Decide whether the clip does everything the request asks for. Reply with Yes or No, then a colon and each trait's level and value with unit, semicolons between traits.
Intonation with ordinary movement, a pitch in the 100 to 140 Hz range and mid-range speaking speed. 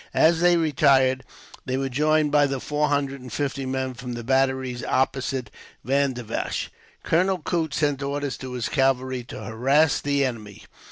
No: narrow, 2.2 semitones; low, 135 Hz; average, 160 wpm